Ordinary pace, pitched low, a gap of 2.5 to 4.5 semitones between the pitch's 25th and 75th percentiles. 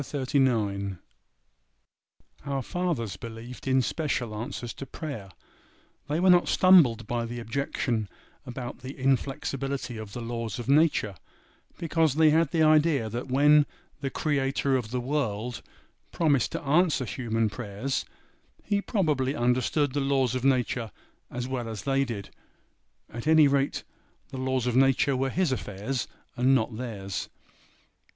Yes: average, 145 wpm; low, 130 Hz; average, 3.4 semitones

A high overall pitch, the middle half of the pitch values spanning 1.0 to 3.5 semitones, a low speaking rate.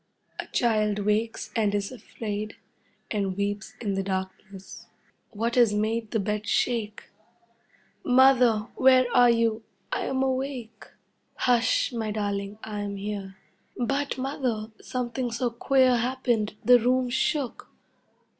Yes: high, 225 Hz; average, 3.2 semitones; slow, 125 wpm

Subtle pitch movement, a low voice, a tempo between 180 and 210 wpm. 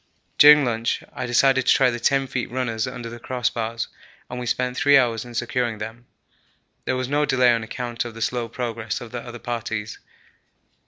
Yes: narrow, 1.6 semitones; low, 120 Hz; average, 195 wpm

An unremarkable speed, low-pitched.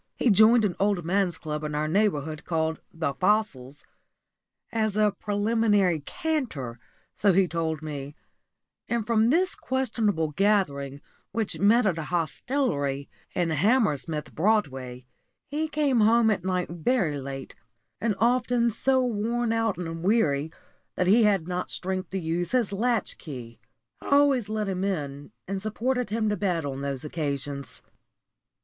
No: average, 145 wpm; high, 190 Hz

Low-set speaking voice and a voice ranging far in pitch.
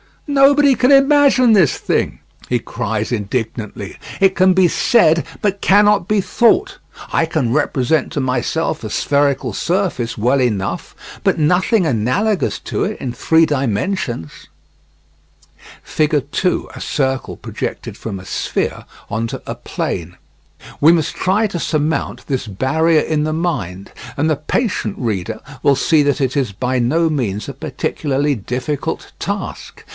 No: medium, 150 Hz; wide, 7.1 semitones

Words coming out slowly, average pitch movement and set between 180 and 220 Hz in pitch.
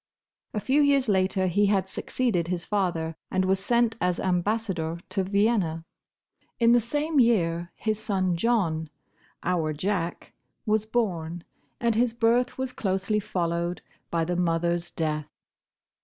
Yes: slow, 130 wpm; average, 4.8 semitones; high, 190 Hz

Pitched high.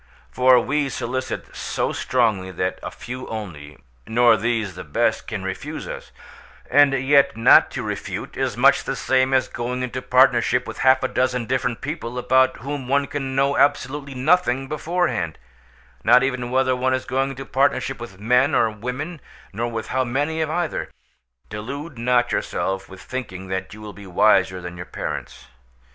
No: low, 125 Hz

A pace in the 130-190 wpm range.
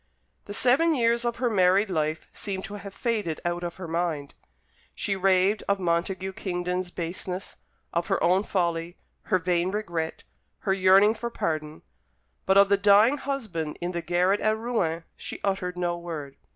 Yes: average, 165 wpm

